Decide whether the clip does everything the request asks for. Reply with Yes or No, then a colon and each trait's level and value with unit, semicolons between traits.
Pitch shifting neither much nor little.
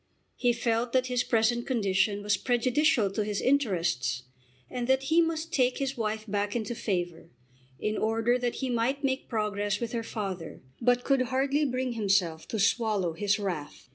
Yes: average, 3.9 semitones